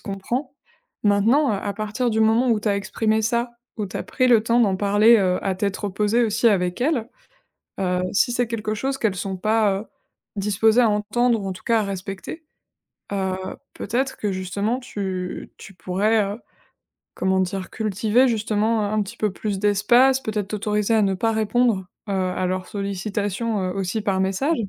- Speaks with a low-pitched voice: No, high, 210 Hz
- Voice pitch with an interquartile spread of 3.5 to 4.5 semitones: No, average, 2.7 semitones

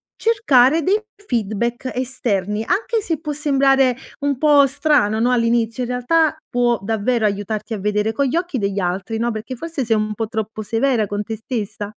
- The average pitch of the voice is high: Yes, high, 235 Hz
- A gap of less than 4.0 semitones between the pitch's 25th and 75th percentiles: No, average, 4.4 semitones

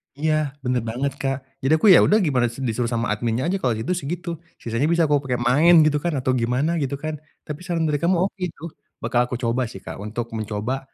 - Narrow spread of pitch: No, average, 4.8 semitones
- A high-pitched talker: No, low, 135 Hz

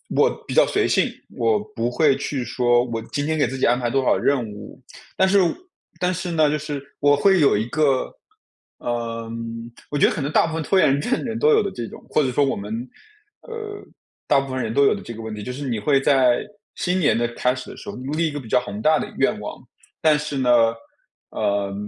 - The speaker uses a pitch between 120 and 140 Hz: Yes, low, 135 Hz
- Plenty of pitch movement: No, average, 4.3 semitones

